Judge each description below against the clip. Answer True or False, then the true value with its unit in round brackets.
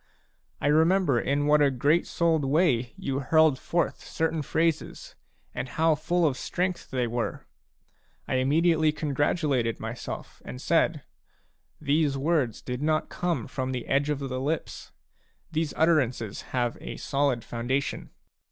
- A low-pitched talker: False (145 Hz)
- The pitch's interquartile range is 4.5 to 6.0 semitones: False (3.8 semitones)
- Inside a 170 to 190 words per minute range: False (145 wpm)